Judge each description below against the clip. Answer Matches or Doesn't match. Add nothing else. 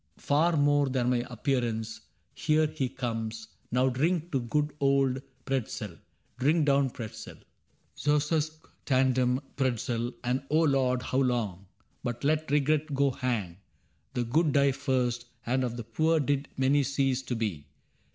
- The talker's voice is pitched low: Matches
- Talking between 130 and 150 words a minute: Matches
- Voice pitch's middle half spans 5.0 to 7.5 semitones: Doesn't match